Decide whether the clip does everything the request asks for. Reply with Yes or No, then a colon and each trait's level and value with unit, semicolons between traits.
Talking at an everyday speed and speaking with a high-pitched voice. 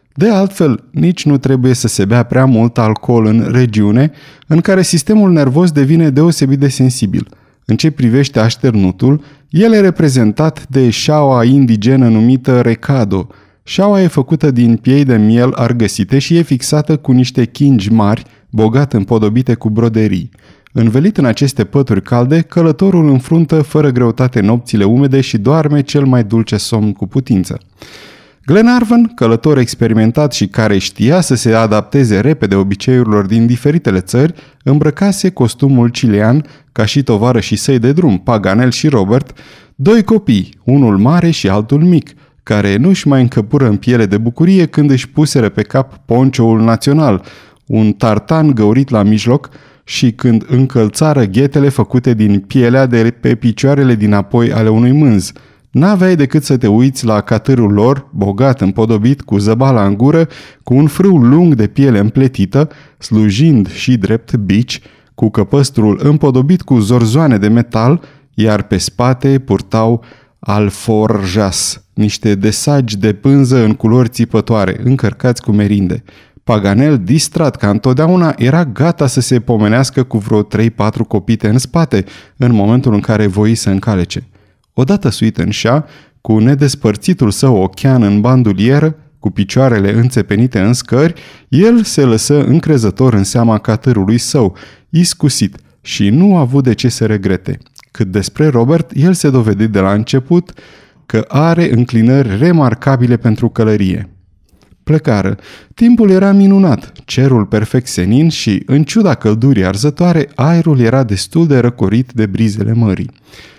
No: average, 145 wpm; low, 125 Hz